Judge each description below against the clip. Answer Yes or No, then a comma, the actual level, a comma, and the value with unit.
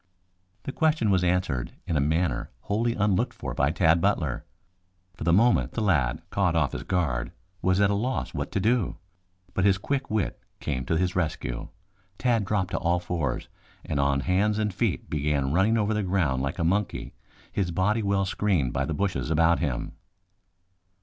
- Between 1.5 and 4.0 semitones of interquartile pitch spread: No, average, 4.9 semitones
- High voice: No, very low, 90 Hz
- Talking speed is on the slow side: No, average, 185 wpm